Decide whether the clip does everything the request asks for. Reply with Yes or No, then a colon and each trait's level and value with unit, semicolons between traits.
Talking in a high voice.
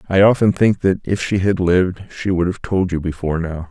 No: very low, 90 Hz